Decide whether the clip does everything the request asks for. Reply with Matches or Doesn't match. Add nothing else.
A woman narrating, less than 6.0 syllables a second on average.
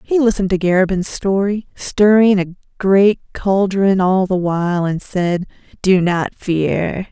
Matches